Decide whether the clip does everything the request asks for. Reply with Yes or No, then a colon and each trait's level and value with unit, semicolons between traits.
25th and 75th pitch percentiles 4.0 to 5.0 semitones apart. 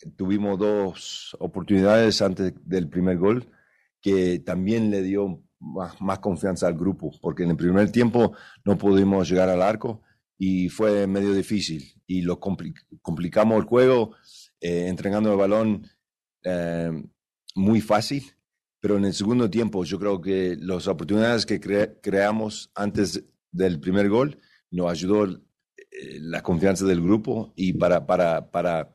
No: narrow, 2.4 semitones